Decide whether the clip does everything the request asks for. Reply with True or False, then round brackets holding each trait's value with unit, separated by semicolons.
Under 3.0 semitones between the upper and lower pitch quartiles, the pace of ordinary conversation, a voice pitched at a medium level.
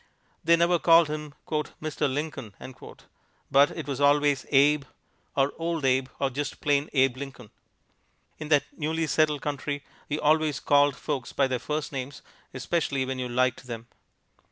True (2.4 semitones; 155 wpm; 145 Hz)